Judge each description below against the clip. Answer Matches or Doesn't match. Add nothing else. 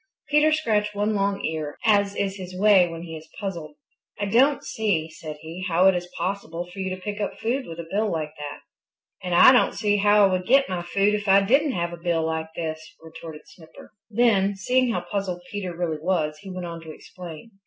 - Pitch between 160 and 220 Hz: Matches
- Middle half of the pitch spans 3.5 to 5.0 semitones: Matches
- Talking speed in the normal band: Doesn't match